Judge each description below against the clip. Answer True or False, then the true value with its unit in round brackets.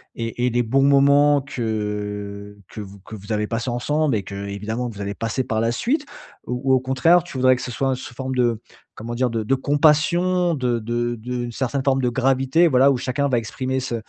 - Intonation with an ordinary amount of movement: True (3.2 semitones)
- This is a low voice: True (125 Hz)